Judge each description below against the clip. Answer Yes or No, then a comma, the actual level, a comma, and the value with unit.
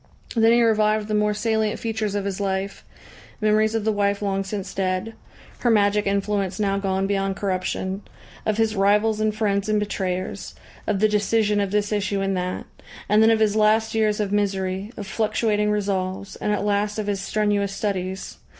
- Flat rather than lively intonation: Yes, narrow, 1.5 semitones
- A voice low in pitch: No, high, 205 Hz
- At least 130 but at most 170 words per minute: No, average, 185 wpm